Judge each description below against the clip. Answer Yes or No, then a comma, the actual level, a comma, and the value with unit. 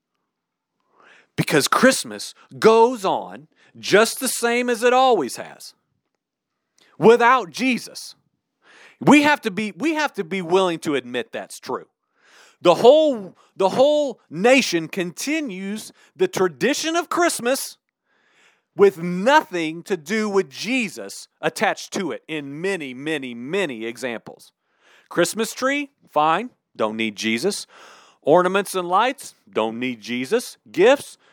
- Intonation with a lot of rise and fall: Yes, wide, 8.0 semitones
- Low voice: No, high, 200 Hz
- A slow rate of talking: Yes, slow, 120 wpm